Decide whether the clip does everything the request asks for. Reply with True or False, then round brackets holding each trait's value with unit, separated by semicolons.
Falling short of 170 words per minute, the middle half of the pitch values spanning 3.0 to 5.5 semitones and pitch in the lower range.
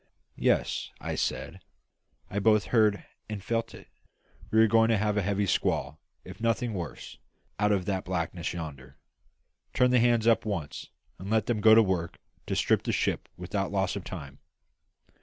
False (175 wpm; 3.7 semitones; 100 Hz)